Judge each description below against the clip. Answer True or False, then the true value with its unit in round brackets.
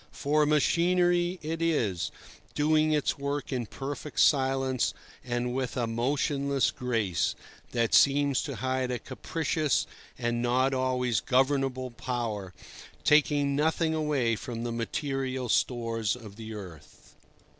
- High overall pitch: False (130 Hz)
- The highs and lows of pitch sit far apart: False (3.6 semitones)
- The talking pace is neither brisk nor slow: False (125 wpm)